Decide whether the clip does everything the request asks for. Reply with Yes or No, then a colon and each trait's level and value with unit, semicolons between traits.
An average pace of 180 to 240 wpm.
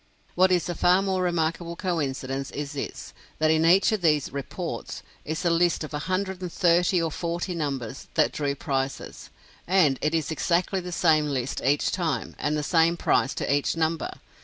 Yes: average, 185 wpm